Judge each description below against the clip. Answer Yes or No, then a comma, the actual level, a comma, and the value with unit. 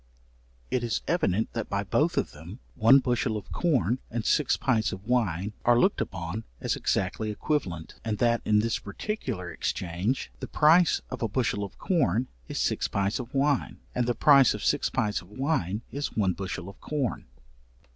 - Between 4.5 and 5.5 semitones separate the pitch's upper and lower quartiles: Yes, average, 4.9 semitones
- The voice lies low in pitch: Yes, low, 115 Hz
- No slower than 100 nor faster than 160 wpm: No, average, 180 wpm